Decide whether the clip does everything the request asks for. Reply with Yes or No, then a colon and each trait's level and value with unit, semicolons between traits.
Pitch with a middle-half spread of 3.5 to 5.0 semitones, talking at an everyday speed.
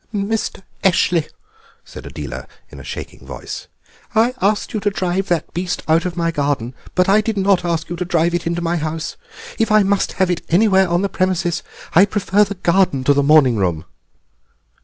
No: average, 3.1 semitones; average, 195 wpm